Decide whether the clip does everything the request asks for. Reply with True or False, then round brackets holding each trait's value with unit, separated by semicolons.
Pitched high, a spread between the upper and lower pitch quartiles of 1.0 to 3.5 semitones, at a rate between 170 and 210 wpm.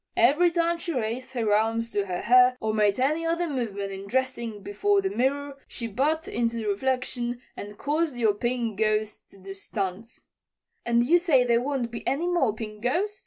False (240 Hz; 4.8 semitones; 190 wpm)